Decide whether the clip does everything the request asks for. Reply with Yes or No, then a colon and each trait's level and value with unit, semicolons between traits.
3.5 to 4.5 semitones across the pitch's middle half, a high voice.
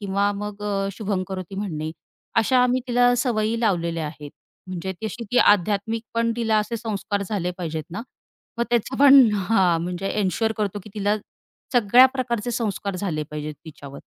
Yes: average, 4.0 semitones; high, 205 Hz